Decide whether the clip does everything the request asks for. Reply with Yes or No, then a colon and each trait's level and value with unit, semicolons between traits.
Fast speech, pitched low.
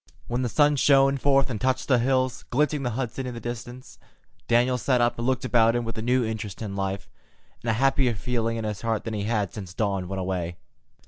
Yes: fast, 235 wpm; low, 120 Hz